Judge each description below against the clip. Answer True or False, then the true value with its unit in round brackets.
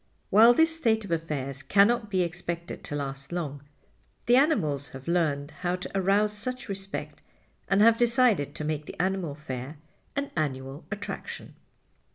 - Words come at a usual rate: True (155 wpm)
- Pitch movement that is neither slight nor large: False (6.5 semitones)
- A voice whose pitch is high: False (180 Hz)